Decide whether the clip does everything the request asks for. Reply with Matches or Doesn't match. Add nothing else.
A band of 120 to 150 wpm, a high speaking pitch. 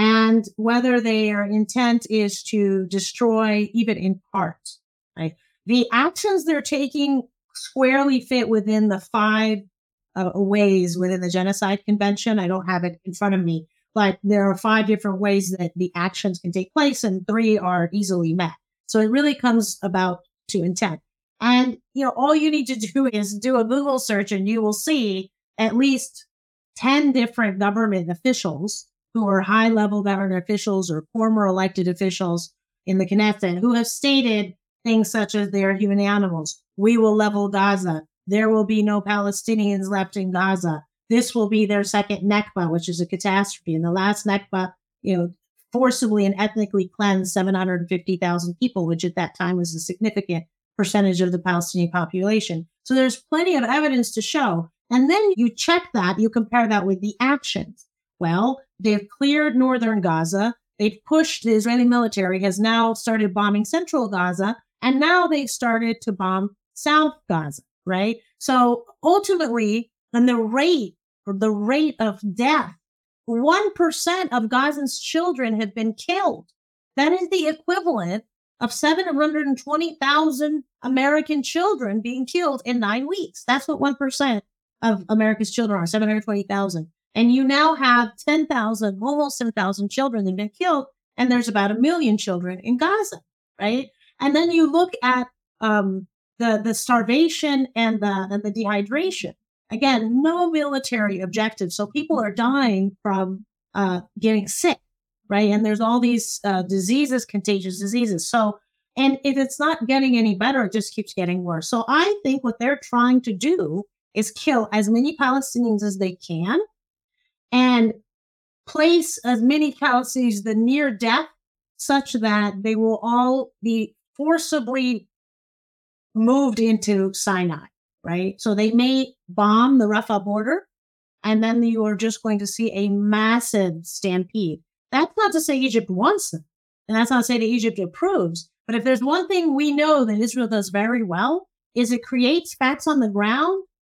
Doesn't match